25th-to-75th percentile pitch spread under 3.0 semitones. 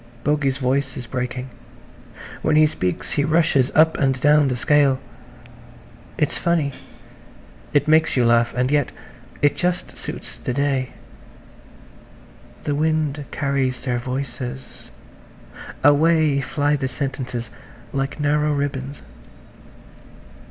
Yes: narrow, 2.5 semitones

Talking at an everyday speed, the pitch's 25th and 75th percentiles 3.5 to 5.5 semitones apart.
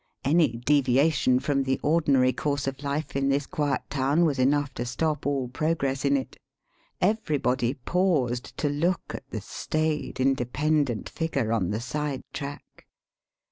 No: average, 145 wpm; narrow, 2.6 semitones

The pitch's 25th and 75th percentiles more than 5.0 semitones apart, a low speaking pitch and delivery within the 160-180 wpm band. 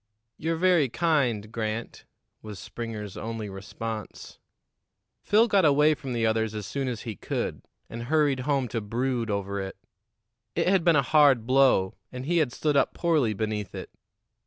Yes: wide, 5.5 semitones; low, 120 Hz; average, 165 wpm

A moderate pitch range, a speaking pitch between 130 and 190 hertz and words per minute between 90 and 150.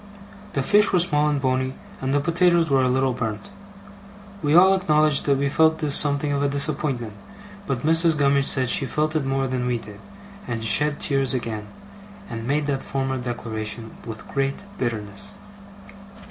No: average, 3.6 semitones; low, 135 Hz; average, 175 wpm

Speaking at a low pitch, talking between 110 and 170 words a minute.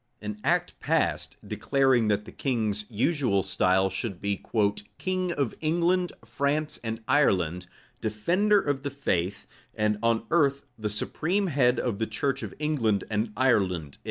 Yes: low, 120 Hz; average, 145 wpm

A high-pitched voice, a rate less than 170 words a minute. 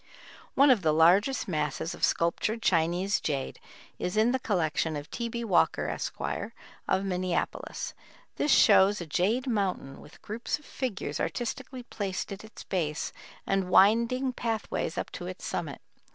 Yes: high, 195 Hz; average, 150 wpm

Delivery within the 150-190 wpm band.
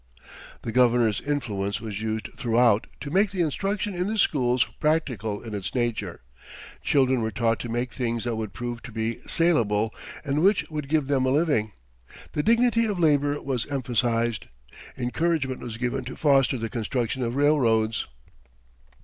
Yes: average, 165 wpm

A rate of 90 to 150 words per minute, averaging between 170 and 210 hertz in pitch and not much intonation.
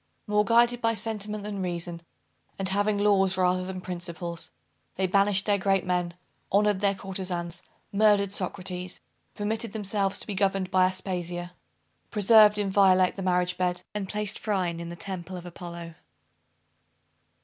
Yes: average, 145 wpm; high, 190 Hz; narrow, 2.3 semitones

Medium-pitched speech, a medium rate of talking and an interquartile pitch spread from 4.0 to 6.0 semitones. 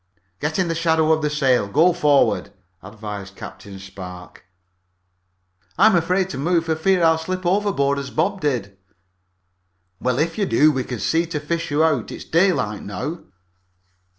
Yes: medium, 155 Hz; average, 160 wpm; average, 5.2 semitones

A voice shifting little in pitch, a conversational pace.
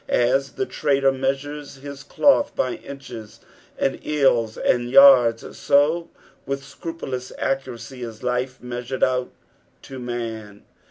No: narrow, 2.2 semitones; slow, 120 wpm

